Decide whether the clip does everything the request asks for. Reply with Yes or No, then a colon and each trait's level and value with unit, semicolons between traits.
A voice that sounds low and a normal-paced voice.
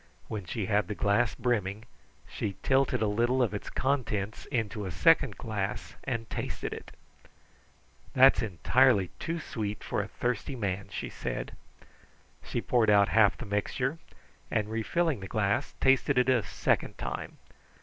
Yes: low, 110 Hz; average, 150 wpm